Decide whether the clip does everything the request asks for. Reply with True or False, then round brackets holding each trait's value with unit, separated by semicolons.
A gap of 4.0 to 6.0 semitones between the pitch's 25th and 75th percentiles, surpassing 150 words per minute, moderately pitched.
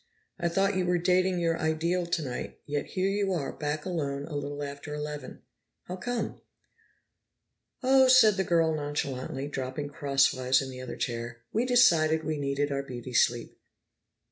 True (4.5 semitones; 160 wpm; 150 Hz)